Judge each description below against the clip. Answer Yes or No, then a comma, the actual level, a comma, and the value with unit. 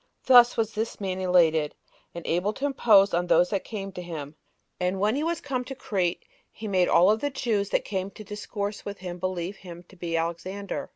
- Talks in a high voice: Yes, high, 195 Hz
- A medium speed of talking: No, fast, 210 wpm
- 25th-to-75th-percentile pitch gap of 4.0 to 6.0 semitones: No, average, 3.3 semitones